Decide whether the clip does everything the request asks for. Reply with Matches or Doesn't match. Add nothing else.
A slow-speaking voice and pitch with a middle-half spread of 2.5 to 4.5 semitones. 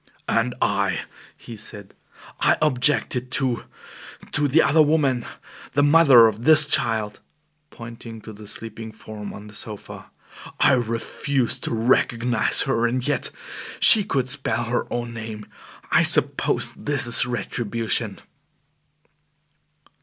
Matches